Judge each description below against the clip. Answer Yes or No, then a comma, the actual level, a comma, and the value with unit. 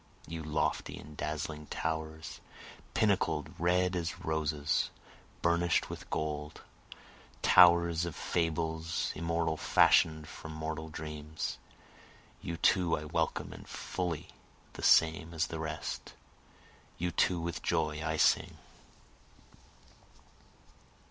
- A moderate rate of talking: No, slow, 105 wpm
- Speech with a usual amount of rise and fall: No, narrow, 1.6 semitones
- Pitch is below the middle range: Yes, very low, 80 Hz